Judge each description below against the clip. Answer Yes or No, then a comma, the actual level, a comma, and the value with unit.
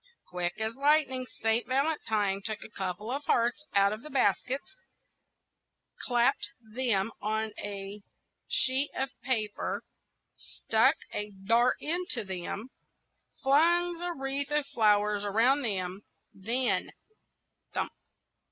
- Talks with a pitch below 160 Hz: No, high, 230 Hz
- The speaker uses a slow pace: Yes, slow, 115 wpm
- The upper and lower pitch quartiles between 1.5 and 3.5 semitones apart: No, average, 4.6 semitones